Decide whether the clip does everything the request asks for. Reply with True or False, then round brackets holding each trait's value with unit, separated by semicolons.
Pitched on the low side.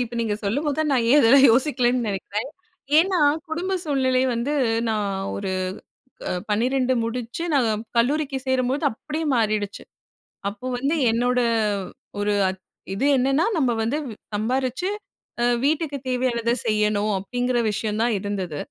False (245 Hz)